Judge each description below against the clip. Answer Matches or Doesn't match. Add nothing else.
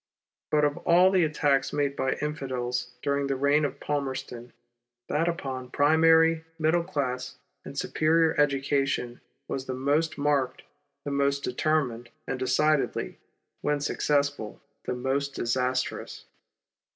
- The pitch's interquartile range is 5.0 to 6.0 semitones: Doesn't match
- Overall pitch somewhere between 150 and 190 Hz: Doesn't match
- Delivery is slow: Matches